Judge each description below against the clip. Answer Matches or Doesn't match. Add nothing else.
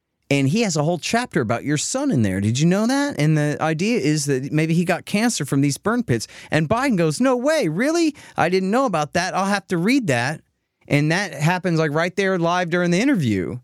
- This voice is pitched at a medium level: Matches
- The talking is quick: Matches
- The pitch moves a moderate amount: Doesn't match